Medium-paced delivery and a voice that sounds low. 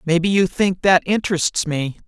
No: average, 175 wpm; medium, 175 Hz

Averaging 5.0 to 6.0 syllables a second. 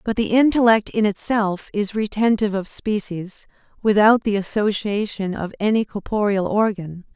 No: 4.8 syllables/s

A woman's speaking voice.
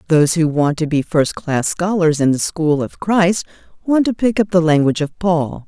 Yes: female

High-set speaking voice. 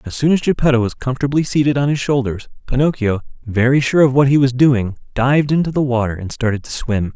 No: low, 130 Hz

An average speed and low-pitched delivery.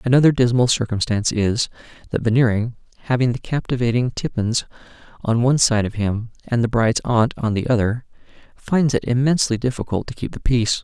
Yes: average, 165 wpm; low, 120 Hz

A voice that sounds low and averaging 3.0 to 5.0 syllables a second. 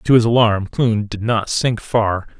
Yes: low, 110 Hz; 4.0 syllables/s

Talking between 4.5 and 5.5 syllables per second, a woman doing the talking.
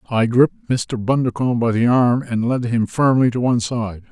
No: 5.4 syllables/s; male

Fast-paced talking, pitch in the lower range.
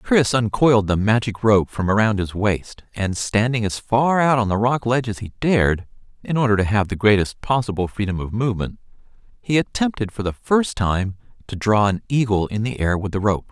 Yes: fast, 210 wpm; low, 110 Hz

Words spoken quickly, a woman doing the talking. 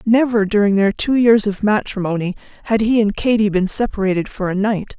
No: average, 195 wpm; female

